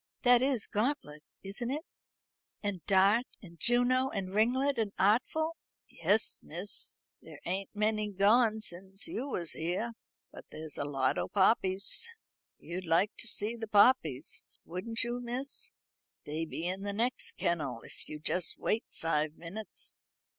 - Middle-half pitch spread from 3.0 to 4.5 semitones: No, wide, 5.5 semitones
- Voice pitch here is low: No, high, 205 Hz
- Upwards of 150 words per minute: No, average, 145 wpm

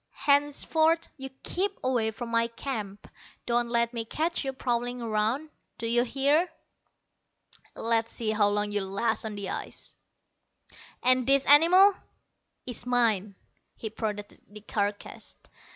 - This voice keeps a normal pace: No, slow, 125 wpm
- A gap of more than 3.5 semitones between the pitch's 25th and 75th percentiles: Yes, average, 4.2 semitones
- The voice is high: Yes, high, 235 Hz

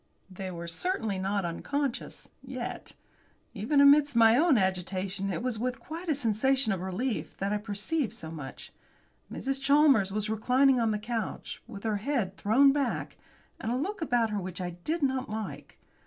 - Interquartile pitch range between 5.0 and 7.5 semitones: Yes, wide, 5.6 semitones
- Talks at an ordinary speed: Yes, average, 170 wpm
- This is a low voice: No, high, 225 Hz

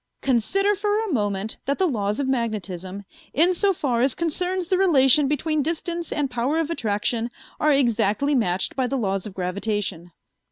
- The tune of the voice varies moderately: No, wide, 7.8 semitones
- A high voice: Yes, very high, 265 Hz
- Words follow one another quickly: No, average, 160 wpm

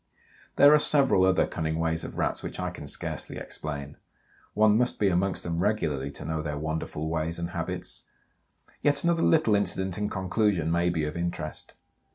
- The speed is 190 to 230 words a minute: No, average, 180 wpm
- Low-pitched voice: Yes, very low, 85 Hz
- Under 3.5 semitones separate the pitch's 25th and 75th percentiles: No, average, 4.7 semitones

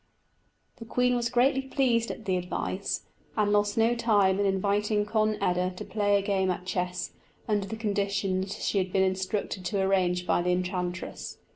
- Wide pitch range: No, narrow, 2.5 semitones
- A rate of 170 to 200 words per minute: Yes, average, 175 wpm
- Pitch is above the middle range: Yes, high, 200 Hz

